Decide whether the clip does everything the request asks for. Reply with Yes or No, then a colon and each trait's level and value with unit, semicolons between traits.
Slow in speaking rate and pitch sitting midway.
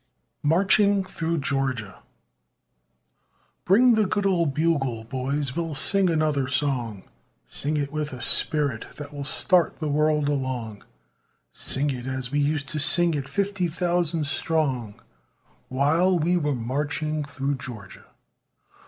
Yes: slow, 130 wpm; medium, 145 Hz